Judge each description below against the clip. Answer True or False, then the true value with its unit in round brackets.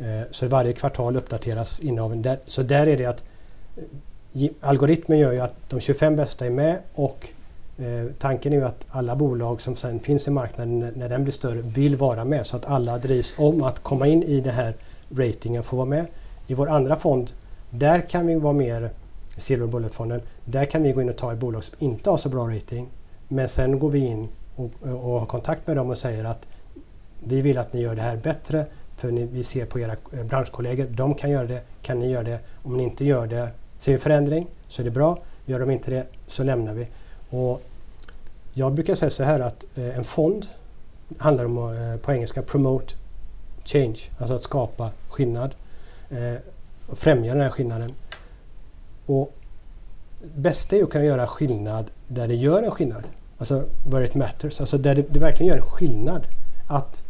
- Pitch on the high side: False (125 Hz)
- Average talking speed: True (185 wpm)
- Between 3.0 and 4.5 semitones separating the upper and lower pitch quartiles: True (3.3 semitones)